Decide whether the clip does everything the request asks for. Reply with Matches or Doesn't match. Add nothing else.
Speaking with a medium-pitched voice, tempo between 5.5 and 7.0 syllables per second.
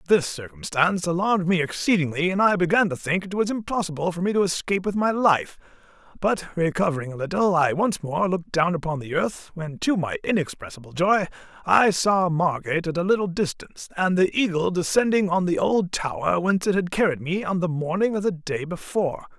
Matches